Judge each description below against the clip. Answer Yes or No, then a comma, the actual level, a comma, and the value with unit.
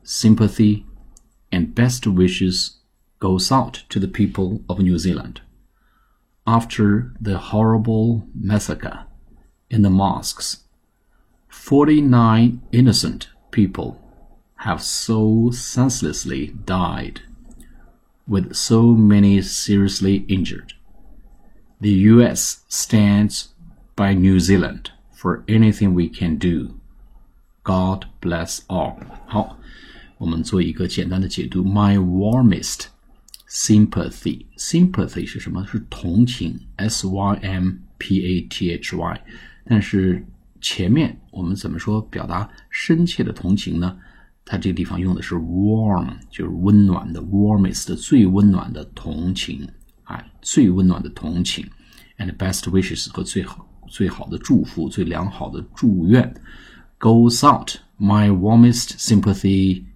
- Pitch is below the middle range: Yes, low, 100 Hz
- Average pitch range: Yes, average, 3.2 semitones